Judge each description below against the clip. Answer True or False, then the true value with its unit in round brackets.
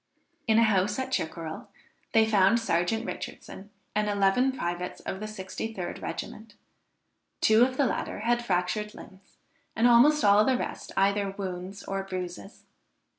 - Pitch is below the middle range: False (205 Hz)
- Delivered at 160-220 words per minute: False (145 wpm)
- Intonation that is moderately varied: True (3.1 semitones)